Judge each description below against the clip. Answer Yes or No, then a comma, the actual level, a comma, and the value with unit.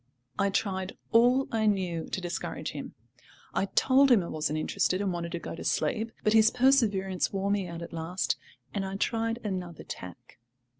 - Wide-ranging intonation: No, average, 4.4 semitones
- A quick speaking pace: No, average, 185 wpm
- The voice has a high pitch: Yes, high, 195 Hz